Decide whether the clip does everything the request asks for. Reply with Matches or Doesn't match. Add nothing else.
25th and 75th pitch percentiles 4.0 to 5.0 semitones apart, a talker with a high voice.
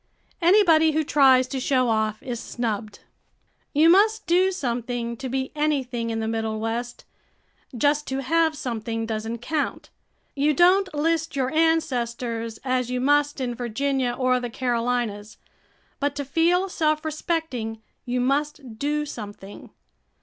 Matches